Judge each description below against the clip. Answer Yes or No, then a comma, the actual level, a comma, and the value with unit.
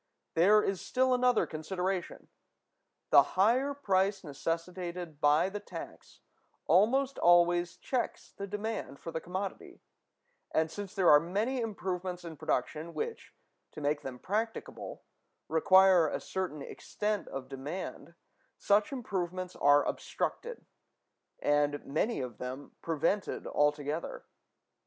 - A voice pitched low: No, medium, 180 Hz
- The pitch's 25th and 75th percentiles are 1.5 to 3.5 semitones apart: No, average, 5.0 semitones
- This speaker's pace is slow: Yes, slow, 120 wpm